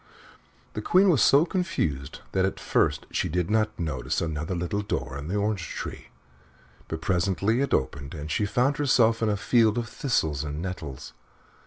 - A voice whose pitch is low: Yes, very low, 95 Hz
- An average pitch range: No, wide, 6.6 semitones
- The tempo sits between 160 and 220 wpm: Yes, average, 175 wpm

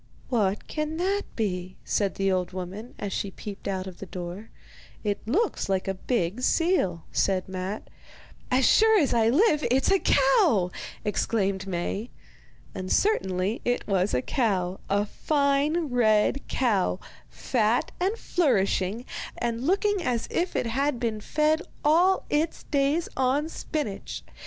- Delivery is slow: No, average, 145 wpm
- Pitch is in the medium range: No, high, 230 Hz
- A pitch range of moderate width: No, wide, 7.5 semitones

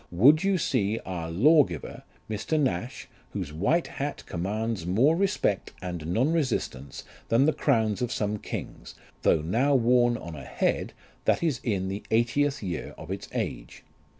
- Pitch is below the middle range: Yes, low, 110 Hz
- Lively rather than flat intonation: Yes, wide, 7.4 semitones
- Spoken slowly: No, average, 160 wpm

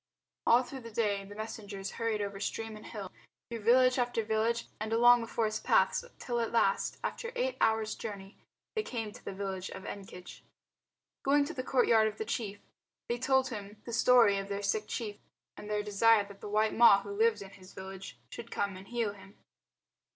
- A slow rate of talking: No, average, 200 wpm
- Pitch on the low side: No, high, 220 Hz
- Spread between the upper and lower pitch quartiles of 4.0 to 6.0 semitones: No, average, 2.9 semitones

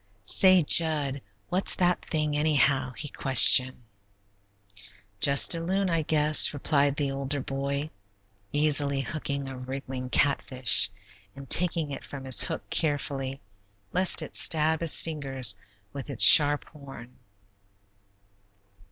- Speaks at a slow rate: Yes, slow, 120 wpm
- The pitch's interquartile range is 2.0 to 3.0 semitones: Yes, narrow, 2.4 semitones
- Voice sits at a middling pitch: Yes, medium, 145 Hz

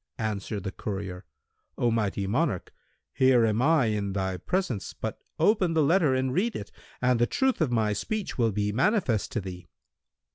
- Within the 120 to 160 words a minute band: No, average, 175 wpm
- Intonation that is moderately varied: No, wide, 7.4 semitones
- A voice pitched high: No, low, 115 Hz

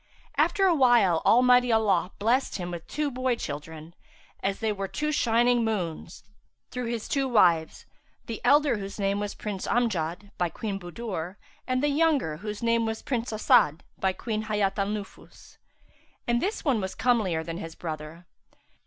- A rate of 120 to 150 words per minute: No, average, 165 wpm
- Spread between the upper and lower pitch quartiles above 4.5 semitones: Yes, average, 5.3 semitones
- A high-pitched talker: Yes, high, 215 Hz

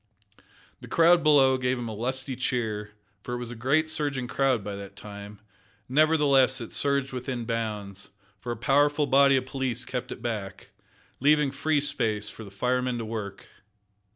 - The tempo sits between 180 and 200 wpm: No, average, 170 wpm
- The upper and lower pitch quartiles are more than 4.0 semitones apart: No, average, 3.7 semitones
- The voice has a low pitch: Yes, low, 125 Hz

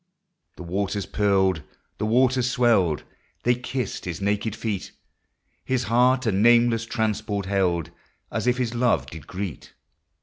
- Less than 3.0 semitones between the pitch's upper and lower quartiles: No, average, 3.9 semitones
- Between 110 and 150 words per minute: Yes, average, 145 wpm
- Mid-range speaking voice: No, low, 110 Hz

